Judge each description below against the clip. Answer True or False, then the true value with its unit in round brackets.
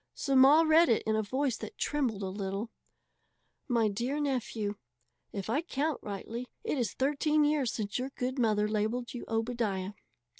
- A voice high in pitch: True (240 Hz)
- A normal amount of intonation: True (4.5 semitones)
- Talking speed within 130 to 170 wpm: True (165 wpm)